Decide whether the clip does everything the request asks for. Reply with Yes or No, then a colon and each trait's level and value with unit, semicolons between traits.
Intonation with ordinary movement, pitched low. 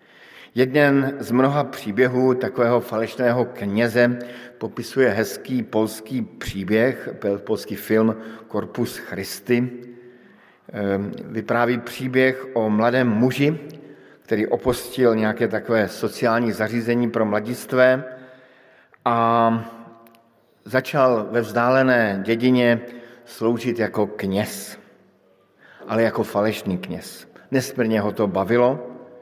No: narrow, 2.2 semitones; low, 120 Hz